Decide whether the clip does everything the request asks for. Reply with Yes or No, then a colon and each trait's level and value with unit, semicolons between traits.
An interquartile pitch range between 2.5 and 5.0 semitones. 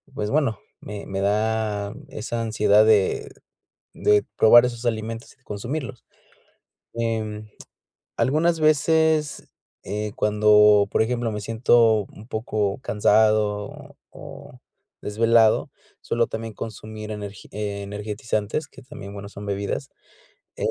No: narrow, 2.1 semitones